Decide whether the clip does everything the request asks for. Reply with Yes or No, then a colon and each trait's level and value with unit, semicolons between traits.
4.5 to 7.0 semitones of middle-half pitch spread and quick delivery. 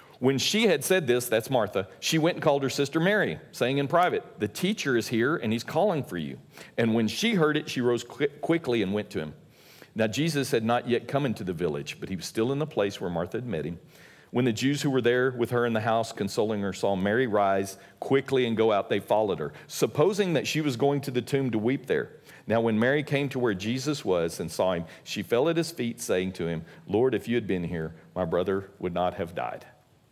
Yes: average, 4.8 semitones; fast, 250 wpm